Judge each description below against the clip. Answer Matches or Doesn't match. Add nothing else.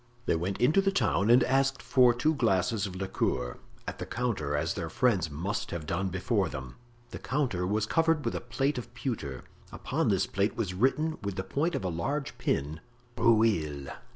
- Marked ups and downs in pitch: Matches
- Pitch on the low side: Matches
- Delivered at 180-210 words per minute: Matches